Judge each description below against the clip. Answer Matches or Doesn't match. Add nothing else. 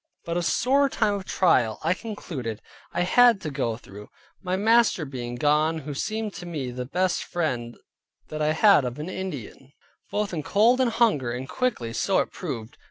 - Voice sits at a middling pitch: Matches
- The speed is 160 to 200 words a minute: Matches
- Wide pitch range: Matches